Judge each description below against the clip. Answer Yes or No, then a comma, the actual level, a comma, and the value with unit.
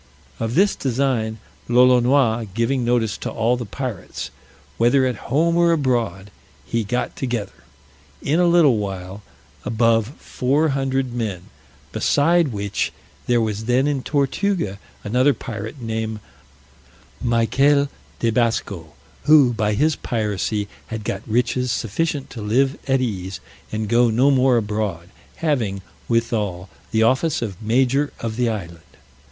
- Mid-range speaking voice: No, low, 120 Hz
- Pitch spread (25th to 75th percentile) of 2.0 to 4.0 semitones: Yes, average, 3.7 semitones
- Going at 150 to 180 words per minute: No, slow, 135 wpm